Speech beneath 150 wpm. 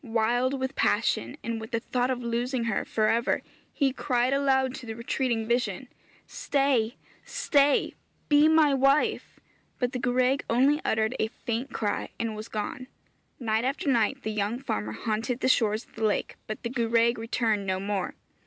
No: average, 170 wpm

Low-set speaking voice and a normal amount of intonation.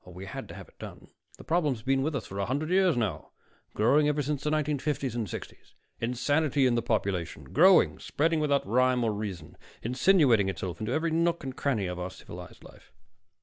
No: low, 130 Hz; wide, 6.4 semitones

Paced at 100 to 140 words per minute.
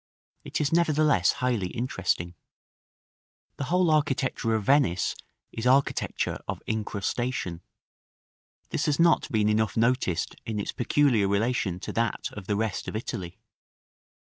Yes: slow, 135 wpm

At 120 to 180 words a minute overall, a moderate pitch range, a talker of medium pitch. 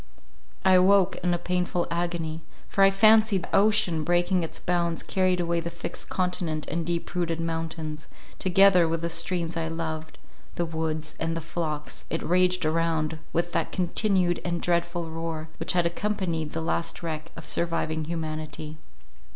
No: average, 155 wpm; narrow, 1.7 semitones; medium, 170 Hz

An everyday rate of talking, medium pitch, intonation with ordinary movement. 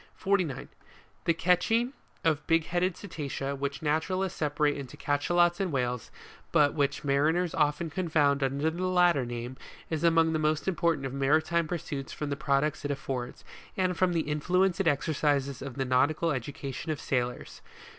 Yes: average, 165 wpm; medium, 150 Hz; average, 3.5 semitones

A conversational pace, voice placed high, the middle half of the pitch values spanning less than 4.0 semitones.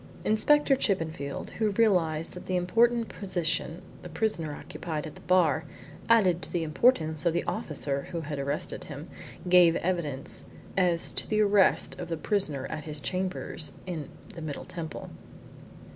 No: average, 155 wpm; medium, 170 Hz; average, 3.5 semitones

